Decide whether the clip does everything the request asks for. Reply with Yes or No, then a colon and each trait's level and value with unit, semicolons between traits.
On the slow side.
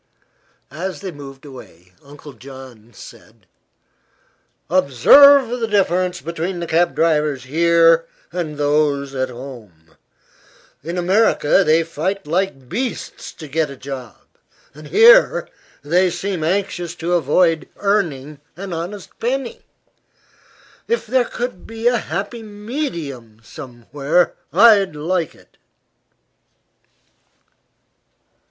Yes: slow, 105 wpm